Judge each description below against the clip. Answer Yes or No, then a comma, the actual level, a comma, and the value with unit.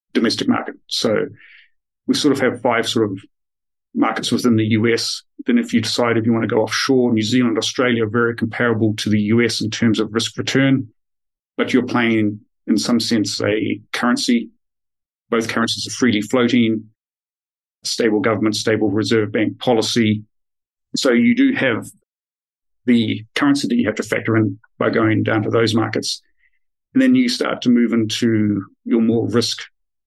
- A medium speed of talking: Yes, average, 170 wpm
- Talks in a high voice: No, low, 115 Hz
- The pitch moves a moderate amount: No, narrow, 2.3 semitones